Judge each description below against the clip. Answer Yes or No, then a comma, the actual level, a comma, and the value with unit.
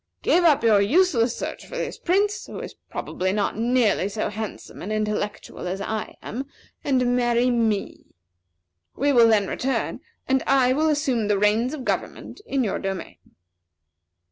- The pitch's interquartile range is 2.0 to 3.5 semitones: No, average, 4.3 semitones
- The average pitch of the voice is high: Yes, high, 235 Hz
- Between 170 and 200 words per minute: No, average, 160 wpm